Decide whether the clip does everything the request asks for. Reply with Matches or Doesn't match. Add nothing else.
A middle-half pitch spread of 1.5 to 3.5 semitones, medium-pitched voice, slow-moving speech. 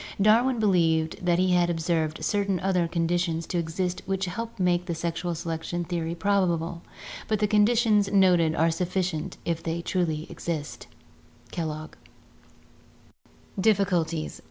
Matches